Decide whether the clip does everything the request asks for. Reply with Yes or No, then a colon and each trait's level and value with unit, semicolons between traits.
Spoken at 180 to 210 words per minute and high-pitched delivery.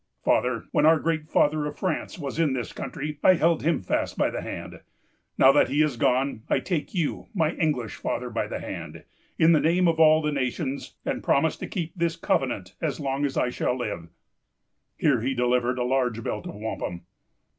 No: average, 200 wpm; medium, 145 Hz